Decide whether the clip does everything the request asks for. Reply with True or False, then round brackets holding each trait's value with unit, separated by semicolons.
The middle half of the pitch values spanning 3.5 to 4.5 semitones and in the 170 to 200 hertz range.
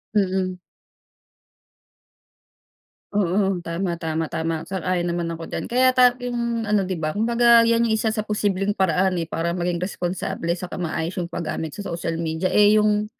True (3.8 semitones; 185 Hz)